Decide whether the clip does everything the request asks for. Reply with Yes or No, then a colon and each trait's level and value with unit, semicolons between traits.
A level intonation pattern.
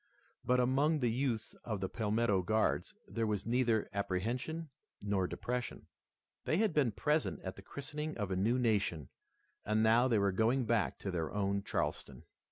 No: average, 4.1 semitones